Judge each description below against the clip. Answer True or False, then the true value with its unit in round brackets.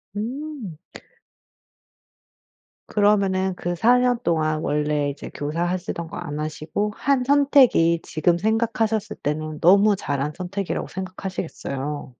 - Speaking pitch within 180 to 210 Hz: True (185 Hz)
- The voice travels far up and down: True (5.7 semitones)